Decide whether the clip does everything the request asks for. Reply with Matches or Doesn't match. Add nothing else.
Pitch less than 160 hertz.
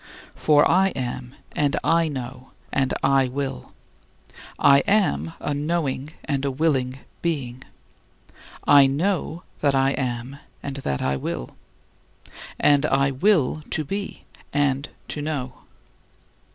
Matches